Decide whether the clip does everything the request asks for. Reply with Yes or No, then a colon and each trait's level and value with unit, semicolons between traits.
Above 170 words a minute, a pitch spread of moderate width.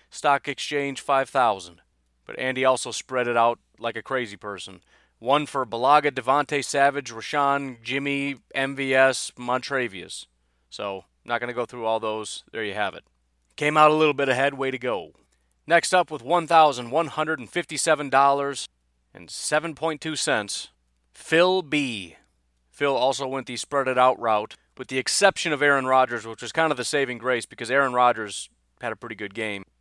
Yes: average, 180 wpm; average, 4.5 semitones